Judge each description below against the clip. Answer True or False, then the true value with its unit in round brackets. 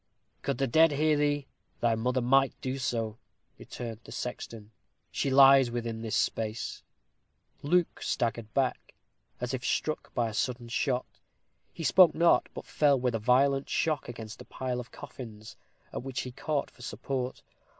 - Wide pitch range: False (2.8 semitones)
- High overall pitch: False (125 Hz)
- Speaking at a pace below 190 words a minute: True (160 wpm)